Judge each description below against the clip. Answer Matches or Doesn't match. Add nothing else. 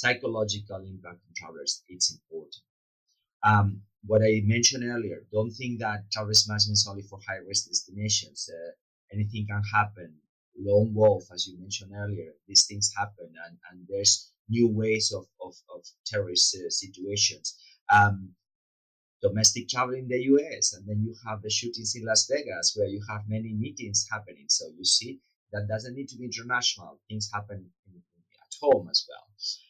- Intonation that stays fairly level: Matches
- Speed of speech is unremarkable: Matches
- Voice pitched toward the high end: Doesn't match